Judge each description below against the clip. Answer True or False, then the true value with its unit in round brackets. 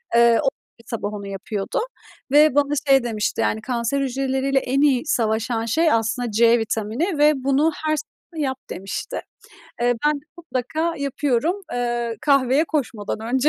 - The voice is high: True (255 Hz)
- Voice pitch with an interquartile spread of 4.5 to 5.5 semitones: False (4.1 semitones)